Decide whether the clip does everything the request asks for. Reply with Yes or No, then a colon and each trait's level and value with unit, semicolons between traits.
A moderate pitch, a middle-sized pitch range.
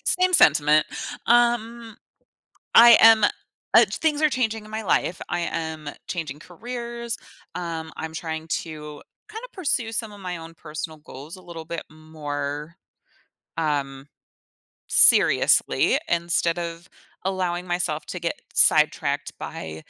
No: medium, 170 Hz; wide, 6.1 semitones